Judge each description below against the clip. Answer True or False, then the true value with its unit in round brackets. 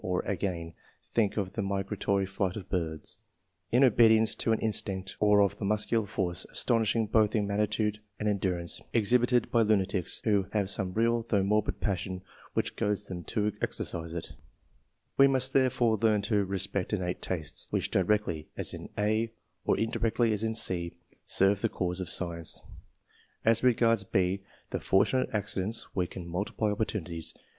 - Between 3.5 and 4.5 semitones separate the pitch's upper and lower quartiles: False (3.1 semitones)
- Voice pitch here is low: True (105 Hz)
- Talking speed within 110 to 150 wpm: False (165 wpm)